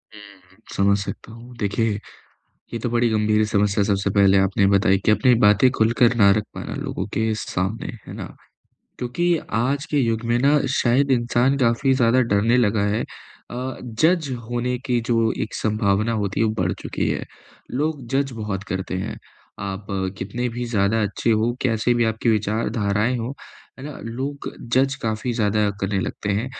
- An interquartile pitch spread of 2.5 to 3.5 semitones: Yes, average, 3.2 semitones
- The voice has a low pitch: Yes, low, 115 Hz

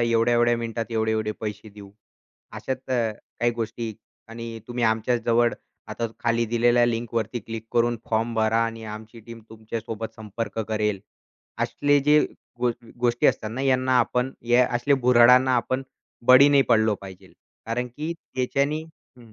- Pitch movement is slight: Yes, narrow, 1.8 semitones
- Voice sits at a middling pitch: No, low, 115 Hz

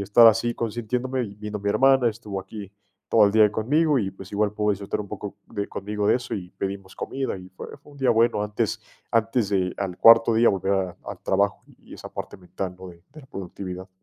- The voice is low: Yes, low, 105 Hz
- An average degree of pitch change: Yes, average, 3.1 semitones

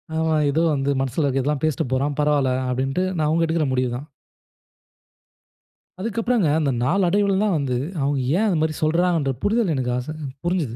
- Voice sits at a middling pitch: Yes, medium, 155 Hz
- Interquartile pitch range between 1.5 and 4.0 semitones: No, average, 4.6 semitones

